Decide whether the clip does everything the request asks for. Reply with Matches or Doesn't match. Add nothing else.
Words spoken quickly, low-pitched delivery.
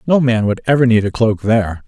Matches